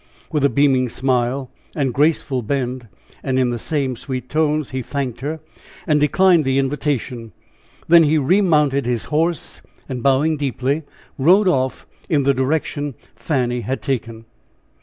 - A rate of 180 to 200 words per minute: No, average, 145 wpm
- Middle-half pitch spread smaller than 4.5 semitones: Yes, average, 2.9 semitones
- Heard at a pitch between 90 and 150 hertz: Yes, low, 135 Hz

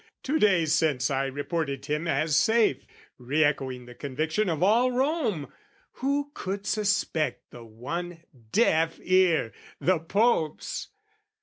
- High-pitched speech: No, medium, 165 Hz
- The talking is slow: Yes, slow, 125 wpm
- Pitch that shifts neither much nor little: No, wide, 6.5 semitones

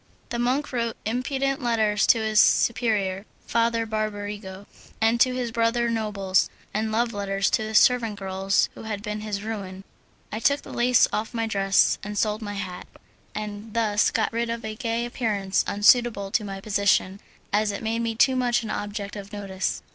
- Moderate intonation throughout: No, narrow, 2.3 semitones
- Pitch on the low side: No, high, 215 Hz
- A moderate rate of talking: Yes, average, 180 wpm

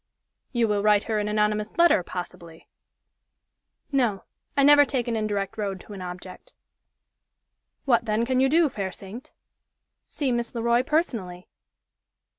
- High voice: Yes, high, 220 Hz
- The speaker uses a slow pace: No, average, 145 wpm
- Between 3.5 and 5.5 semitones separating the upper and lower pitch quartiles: Yes, average, 4.4 semitones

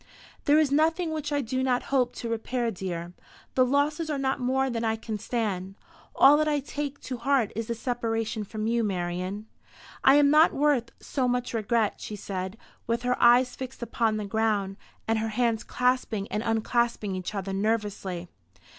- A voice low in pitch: No, high, 235 Hz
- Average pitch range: Yes, average, 3.8 semitones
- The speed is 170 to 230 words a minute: Yes, average, 180 wpm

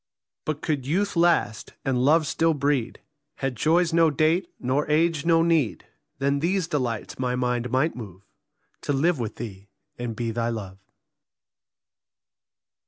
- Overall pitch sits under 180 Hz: Yes, medium, 140 Hz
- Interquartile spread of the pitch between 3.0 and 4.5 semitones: No, average, 5.3 semitones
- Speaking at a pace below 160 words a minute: Yes, average, 145 wpm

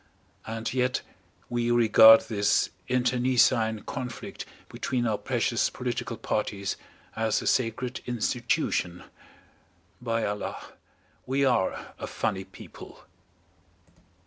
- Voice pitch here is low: Yes, low, 115 Hz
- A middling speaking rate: No, slow, 95 wpm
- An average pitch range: No, narrow, 2.1 semitones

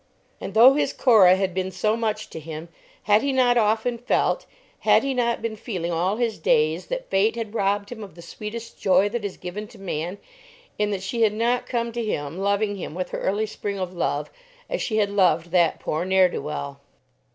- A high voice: Yes, high, 205 Hz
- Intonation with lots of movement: No, average, 3.9 semitones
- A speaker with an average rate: No, fast, 215 wpm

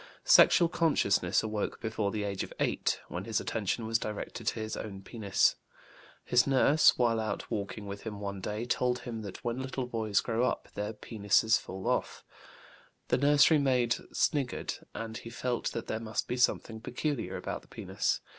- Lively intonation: No, average, 3.1 semitones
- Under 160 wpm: No, average, 175 wpm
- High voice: No, low, 115 Hz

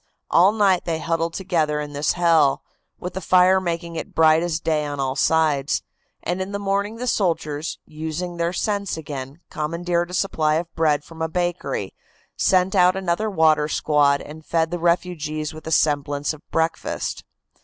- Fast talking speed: No, average, 175 wpm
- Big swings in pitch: No, average, 2.8 semitones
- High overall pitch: No, medium, 165 Hz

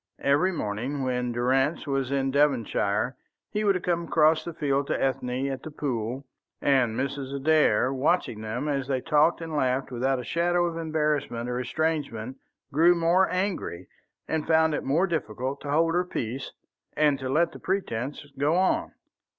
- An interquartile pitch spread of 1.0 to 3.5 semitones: No, average, 4.0 semitones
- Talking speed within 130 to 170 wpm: Yes, average, 165 wpm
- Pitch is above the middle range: No, medium, 140 Hz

